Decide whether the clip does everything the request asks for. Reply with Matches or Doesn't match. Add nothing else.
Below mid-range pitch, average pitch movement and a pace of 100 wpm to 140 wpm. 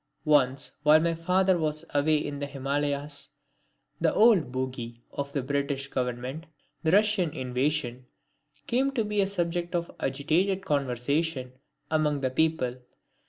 Doesn't match